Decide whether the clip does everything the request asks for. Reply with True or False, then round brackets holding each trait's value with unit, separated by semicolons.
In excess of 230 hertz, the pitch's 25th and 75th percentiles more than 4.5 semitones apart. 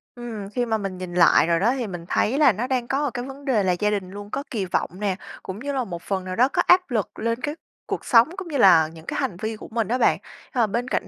False (220 Hz; 5.1 semitones)